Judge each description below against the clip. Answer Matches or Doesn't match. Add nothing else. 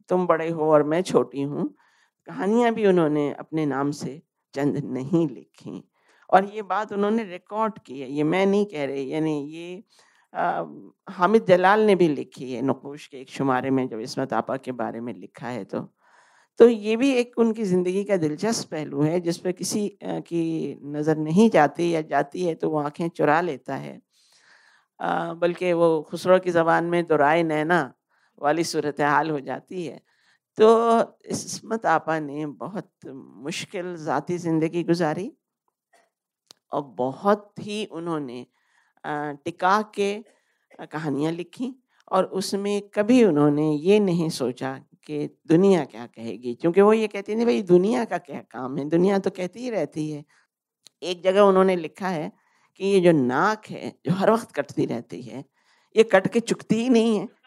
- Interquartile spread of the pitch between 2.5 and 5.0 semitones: Doesn't match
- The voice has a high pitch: Doesn't match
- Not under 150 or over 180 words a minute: Matches